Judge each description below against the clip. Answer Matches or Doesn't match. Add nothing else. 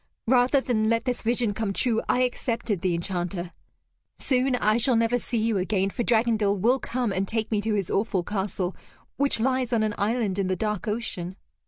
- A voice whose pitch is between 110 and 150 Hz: Doesn't match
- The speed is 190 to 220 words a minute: Matches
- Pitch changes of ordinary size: Matches